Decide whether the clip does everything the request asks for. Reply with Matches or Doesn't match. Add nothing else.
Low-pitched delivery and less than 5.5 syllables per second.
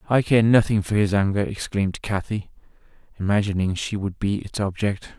Matches